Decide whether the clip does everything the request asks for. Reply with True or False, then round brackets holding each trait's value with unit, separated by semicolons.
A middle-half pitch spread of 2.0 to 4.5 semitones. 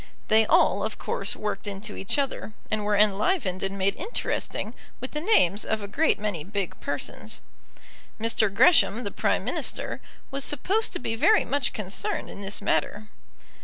False (4.9 semitones)